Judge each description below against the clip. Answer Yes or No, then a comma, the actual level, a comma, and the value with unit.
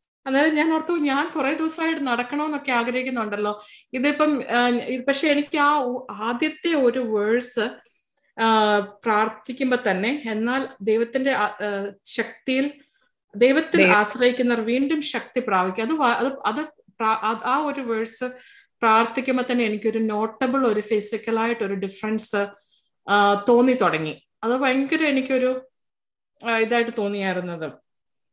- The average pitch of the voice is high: Yes, high, 240 Hz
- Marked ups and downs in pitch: No, average, 3.7 semitones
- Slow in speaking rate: No, average, 95 wpm